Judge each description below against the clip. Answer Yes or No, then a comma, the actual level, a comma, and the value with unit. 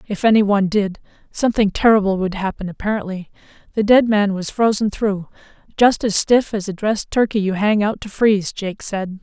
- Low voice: No, high, 205 Hz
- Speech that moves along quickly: No, average, 190 wpm